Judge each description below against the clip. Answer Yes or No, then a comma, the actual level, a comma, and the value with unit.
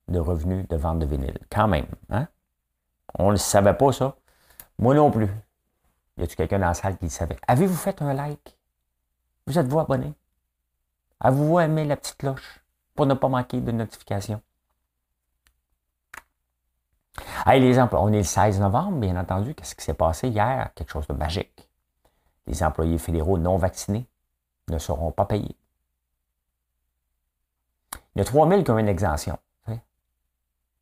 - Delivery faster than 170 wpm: No, average, 160 wpm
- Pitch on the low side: Yes, very low, 85 Hz